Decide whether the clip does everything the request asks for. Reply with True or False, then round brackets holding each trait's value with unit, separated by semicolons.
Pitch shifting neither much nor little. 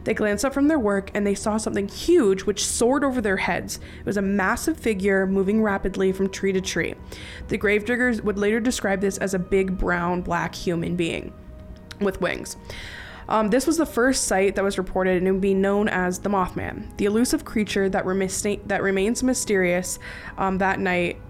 False (2.3 semitones)